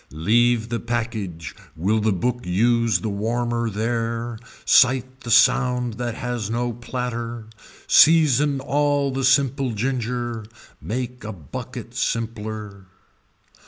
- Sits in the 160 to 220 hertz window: No, low, 120 Hz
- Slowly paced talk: Yes, slow, 115 wpm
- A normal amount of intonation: No, narrow, 2.2 semitones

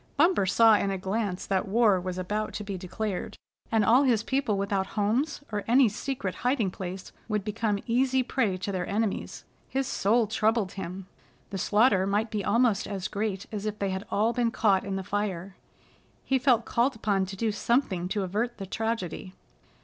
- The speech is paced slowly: No, average, 190 wpm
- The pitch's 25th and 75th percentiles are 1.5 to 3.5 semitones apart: Yes, average, 3.1 semitones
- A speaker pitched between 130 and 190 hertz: No, high, 210 Hz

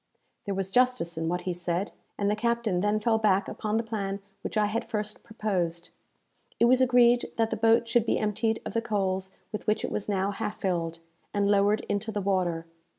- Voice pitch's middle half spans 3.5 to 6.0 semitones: No, average, 2.8 semitones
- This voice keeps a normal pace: No, fast, 210 wpm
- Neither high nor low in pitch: No, high, 210 Hz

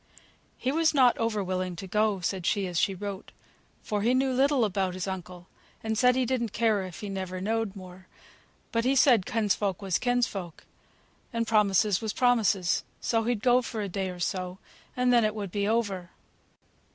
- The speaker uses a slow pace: No, average, 190 wpm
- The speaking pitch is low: No, high, 210 Hz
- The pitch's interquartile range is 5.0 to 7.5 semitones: No, average, 3.9 semitones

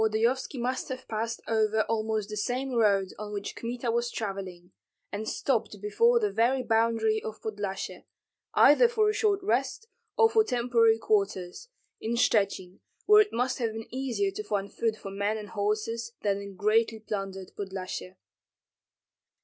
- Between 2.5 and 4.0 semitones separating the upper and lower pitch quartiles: Yes, average, 3.3 semitones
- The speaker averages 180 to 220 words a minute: No, average, 155 wpm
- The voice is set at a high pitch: Yes, high, 220 Hz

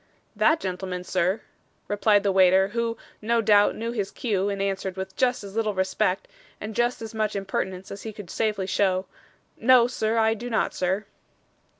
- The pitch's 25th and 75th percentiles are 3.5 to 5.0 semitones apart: No, average, 2.8 semitones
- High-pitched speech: Yes, high, 205 Hz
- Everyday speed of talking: Yes, average, 180 wpm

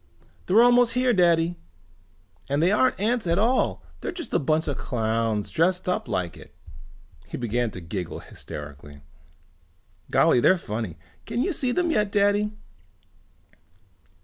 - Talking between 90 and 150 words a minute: Yes, average, 145 wpm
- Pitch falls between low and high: Yes, medium, 175 Hz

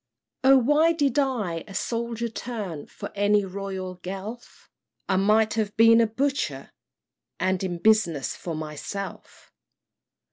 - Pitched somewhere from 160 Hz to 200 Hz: No, high, 210 Hz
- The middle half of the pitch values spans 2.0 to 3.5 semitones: No, average, 4.0 semitones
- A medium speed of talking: No, slow, 130 wpm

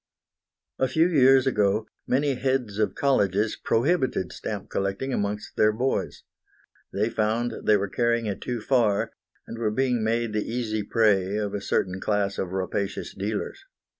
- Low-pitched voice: Yes, low, 110 Hz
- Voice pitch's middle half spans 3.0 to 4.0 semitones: Yes, average, 3.6 semitones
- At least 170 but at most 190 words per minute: No, average, 155 wpm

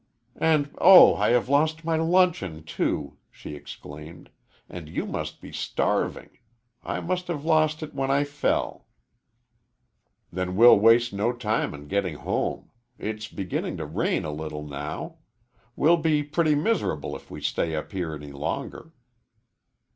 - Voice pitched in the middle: No, low, 120 Hz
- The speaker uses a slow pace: No, average, 145 wpm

